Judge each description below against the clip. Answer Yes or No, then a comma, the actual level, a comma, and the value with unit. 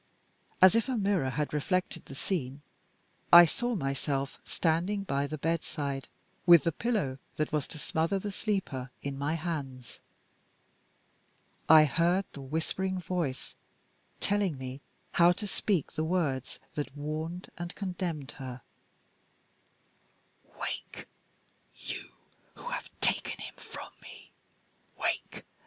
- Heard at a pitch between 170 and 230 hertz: No, medium, 160 Hz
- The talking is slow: Yes, slow, 125 wpm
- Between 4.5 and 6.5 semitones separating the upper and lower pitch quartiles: Yes, average, 4.8 semitones